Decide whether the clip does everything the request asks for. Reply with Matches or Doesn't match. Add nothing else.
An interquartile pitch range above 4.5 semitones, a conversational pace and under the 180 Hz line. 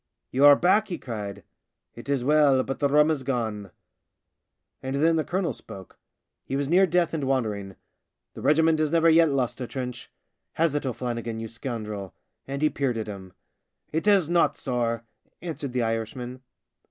Matches